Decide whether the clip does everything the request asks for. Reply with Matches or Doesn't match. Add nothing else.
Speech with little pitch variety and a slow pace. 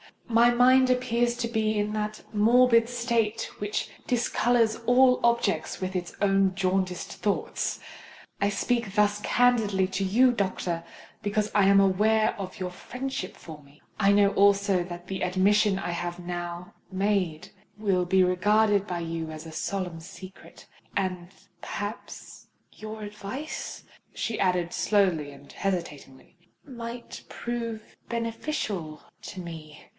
Doesn't match